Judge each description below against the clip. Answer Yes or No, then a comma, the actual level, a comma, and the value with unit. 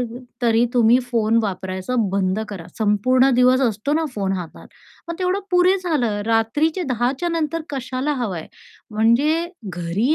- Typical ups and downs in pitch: No, wide, 6.4 semitones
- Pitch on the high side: Yes, high, 240 Hz